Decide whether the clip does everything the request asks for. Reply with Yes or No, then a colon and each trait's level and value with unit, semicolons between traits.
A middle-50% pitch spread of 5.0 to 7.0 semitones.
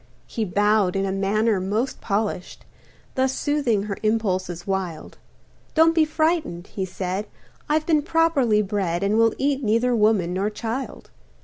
Yes: average, 5.3 semitones